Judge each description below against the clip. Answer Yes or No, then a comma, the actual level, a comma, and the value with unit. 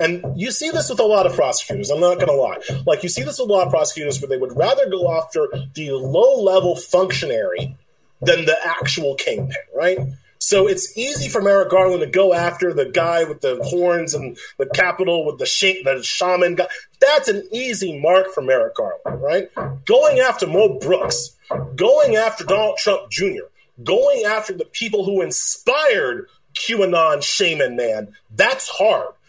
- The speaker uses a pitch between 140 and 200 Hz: Yes, high, 190 Hz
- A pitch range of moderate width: No, wide, 8.4 semitones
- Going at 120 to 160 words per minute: No, average, 180 wpm